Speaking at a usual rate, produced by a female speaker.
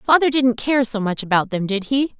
No: fast, 245 wpm; female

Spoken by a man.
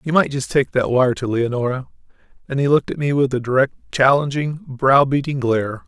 Yes: male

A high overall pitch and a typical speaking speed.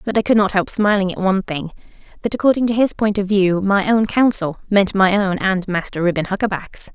No: high, 195 Hz; fast, 225 wpm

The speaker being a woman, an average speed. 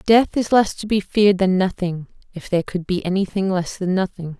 No: female; fast, 220 wpm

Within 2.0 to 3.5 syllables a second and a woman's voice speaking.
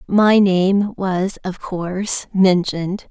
Yes: 3.2 syllables/s; female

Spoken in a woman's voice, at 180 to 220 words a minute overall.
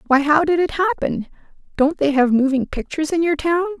Yes: female; fast, 205 wpm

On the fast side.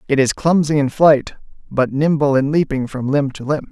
Yes: fast, 210 wpm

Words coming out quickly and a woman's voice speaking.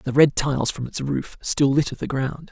No: fast, 240 wpm; male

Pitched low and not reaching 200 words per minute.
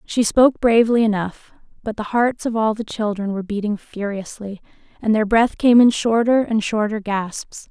No: high, 220 Hz; average, 180 wpm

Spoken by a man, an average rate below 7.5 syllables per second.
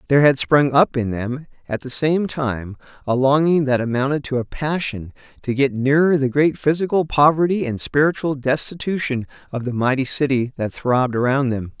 Yes: male; 5.2 syllables/s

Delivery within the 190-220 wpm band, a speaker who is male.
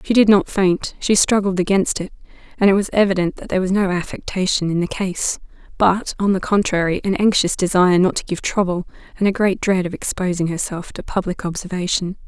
No: average, 200 wpm; female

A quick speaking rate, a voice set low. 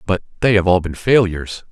Yes: fast, 210 wpm; very low, 95 Hz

